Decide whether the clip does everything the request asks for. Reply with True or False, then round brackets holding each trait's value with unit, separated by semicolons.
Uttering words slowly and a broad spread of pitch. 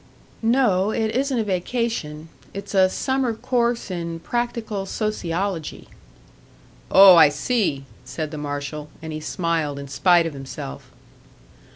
True (130 wpm; 6.7 semitones)